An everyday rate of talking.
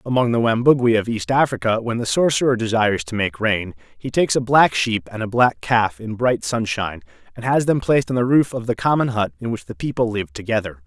No: fast, 230 wpm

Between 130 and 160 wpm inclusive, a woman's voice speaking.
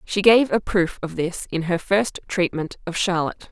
No: fast, 205 wpm; female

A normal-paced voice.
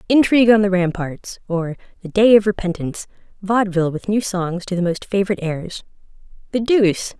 Yes: average, 165 wpm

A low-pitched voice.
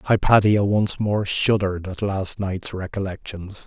Yes: low, 100 Hz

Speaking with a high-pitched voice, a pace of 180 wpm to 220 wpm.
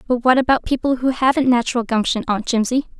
Yes: high, 245 Hz; average, 200 wpm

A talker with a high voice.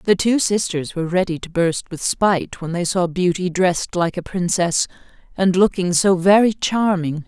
No: medium, 180 Hz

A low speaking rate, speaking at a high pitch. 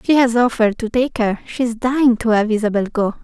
No: fast, 205 wpm; high, 230 Hz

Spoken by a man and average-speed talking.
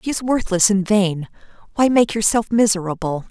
No: female; average, 165 wpm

